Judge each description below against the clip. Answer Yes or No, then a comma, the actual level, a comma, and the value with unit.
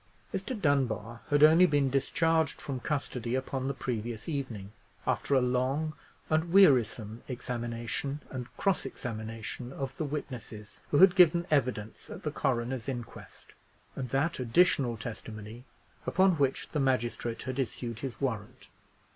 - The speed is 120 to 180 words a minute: Yes, average, 140 wpm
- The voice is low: Yes, low, 130 Hz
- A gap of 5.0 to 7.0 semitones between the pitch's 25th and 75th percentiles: No, average, 3.8 semitones